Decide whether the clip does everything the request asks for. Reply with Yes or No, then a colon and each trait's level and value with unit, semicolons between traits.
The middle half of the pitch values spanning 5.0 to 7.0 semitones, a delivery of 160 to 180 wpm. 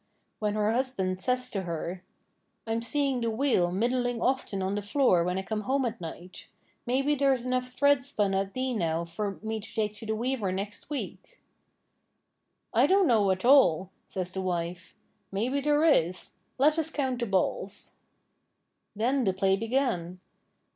Yes: wide, 5.4 semitones; average, 170 wpm